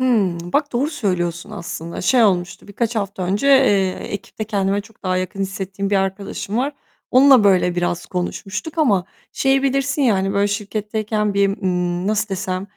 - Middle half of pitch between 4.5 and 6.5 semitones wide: No, average, 3.3 semitones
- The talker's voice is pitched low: No, high, 200 Hz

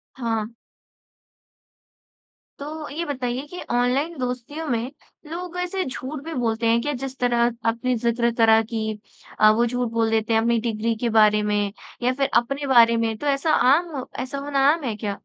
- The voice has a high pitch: Yes, high, 245 Hz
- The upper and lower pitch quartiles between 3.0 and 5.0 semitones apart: Yes, average, 3.7 semitones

